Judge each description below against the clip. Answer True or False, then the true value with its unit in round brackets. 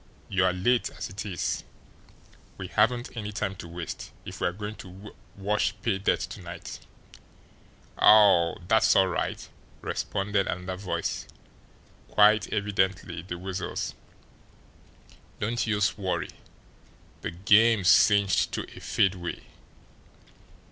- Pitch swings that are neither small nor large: False (2.3 semitones)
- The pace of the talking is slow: True (115 wpm)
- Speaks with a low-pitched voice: True (100 Hz)